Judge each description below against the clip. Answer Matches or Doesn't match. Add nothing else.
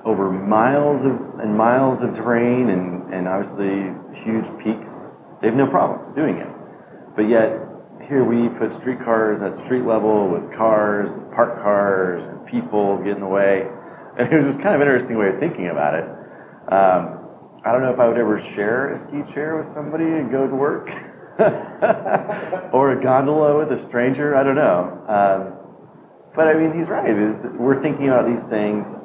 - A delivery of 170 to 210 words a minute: Matches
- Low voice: Matches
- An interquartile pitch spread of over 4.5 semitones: Matches